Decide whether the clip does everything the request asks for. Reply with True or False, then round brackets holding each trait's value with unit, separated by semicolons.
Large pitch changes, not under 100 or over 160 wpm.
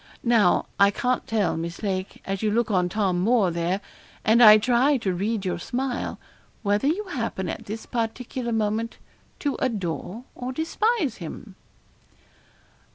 False (4.4 semitones; 150 wpm)